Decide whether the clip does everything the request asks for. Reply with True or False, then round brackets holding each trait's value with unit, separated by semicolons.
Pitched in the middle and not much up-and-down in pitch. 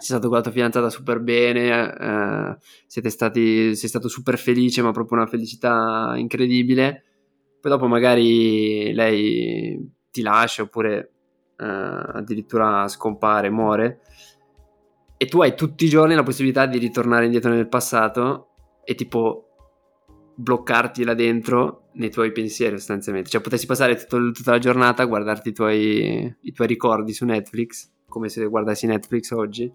False (115 Hz; 2.1 semitones)